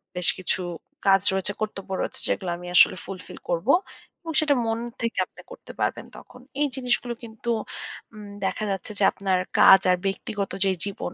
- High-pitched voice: Yes, high, 195 Hz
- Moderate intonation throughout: Yes, average, 3.3 semitones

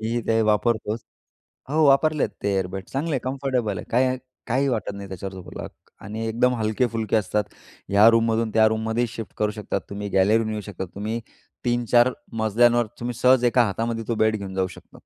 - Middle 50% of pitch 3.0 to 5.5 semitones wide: No, narrow, 2.5 semitones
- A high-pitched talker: No, low, 115 Hz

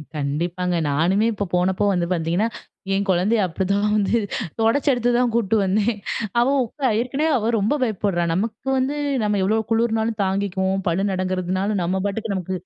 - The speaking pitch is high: Yes, high, 200 Hz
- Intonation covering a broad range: No, average, 3.4 semitones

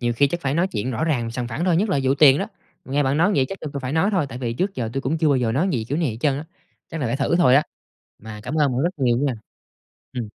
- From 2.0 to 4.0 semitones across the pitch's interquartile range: No, average, 4.4 semitones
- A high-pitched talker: No, medium, 140 Hz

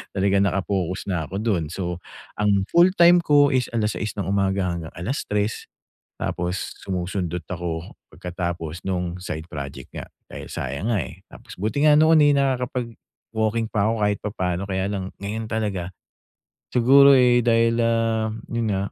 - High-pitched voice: No, low, 100 Hz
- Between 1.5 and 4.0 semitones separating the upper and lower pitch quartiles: No, average, 4.5 semitones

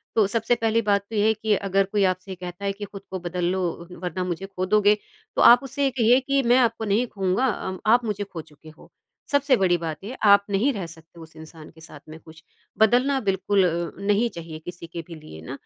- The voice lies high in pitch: Yes, high, 195 Hz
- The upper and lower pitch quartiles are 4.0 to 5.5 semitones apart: Yes, average, 4.3 semitones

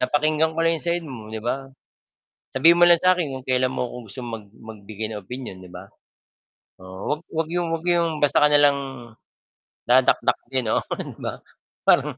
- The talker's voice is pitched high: No, low, 135 Hz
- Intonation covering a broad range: Yes, wide, 5.8 semitones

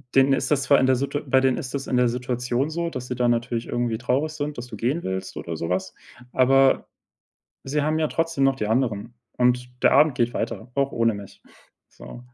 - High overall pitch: No, low, 125 Hz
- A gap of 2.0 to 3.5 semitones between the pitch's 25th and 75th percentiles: Yes, average, 2.7 semitones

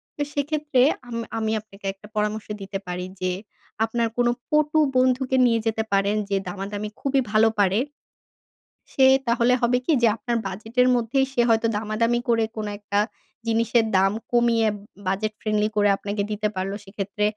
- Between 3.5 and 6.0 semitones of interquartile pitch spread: No, average, 2.8 semitones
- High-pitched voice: Yes, high, 220 Hz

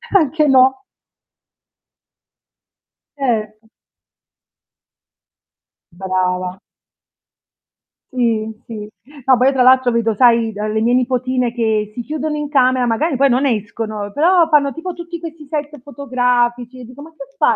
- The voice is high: Yes, very high, 250 Hz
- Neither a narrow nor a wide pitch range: Yes, average, 4.1 semitones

